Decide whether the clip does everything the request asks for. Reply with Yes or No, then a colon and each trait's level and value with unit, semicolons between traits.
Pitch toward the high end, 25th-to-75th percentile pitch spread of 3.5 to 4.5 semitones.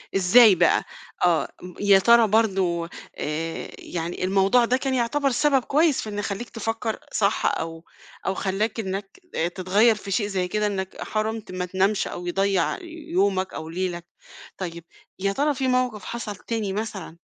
Yes: high, 200 Hz; average, 3.8 semitones